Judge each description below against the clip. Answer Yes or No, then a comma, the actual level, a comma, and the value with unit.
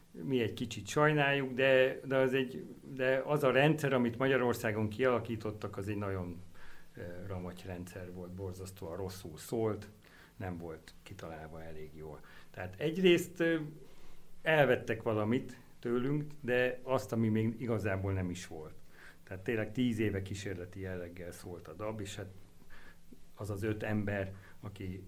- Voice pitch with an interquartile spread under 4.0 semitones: No, wide, 5.5 semitones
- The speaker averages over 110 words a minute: Yes, average, 140 wpm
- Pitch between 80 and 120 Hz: Yes, low, 105 Hz